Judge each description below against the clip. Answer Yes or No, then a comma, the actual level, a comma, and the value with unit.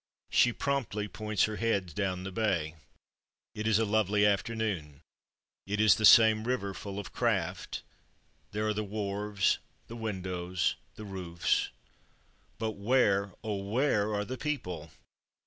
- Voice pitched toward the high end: No, low, 105 Hz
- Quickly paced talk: No, average, 140 wpm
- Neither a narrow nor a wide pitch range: No, narrow, 2.3 semitones